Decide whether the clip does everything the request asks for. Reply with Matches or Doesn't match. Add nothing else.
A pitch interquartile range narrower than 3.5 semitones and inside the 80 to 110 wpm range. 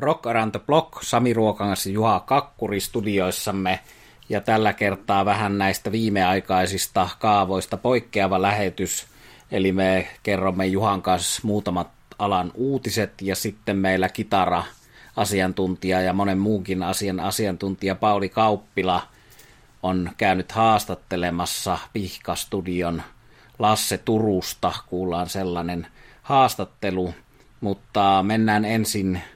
Matches